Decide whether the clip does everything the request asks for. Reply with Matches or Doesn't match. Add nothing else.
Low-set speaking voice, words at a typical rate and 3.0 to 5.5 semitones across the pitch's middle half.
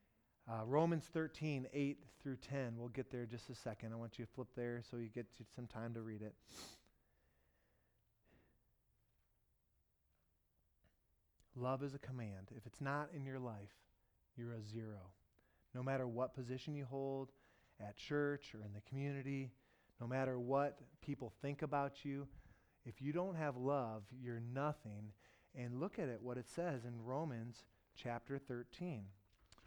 Matches